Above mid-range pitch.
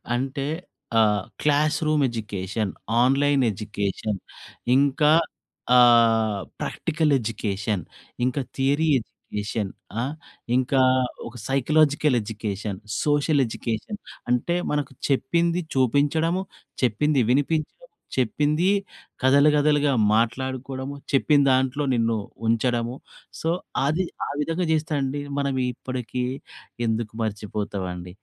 No: low, 130 Hz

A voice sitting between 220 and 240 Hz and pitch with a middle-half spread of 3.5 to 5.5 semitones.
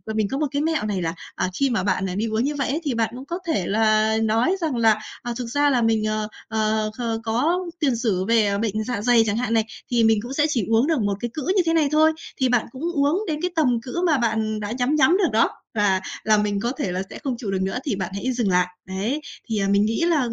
Yes: high, 230 Hz; average, 4.5 semitones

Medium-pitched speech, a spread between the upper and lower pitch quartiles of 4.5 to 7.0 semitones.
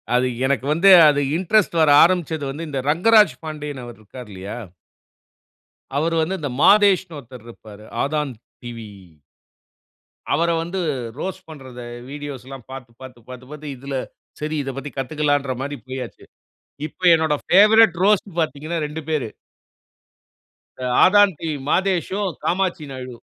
Yes: medium, 150 Hz; average, 4.9 semitones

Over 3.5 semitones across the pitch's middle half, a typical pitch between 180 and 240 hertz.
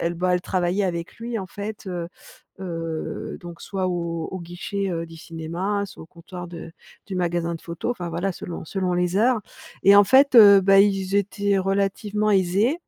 No: average, 2.8 semitones; medium, 185 Hz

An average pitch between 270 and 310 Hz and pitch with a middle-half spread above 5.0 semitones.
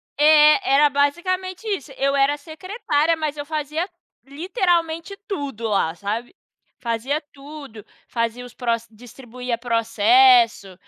Yes: very high, 285 Hz; wide, 5.5 semitones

